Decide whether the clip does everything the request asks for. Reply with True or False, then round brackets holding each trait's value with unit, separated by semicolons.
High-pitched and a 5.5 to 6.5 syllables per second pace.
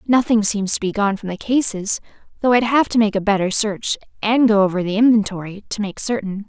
True (210 Hz; 5.7 syllables/s)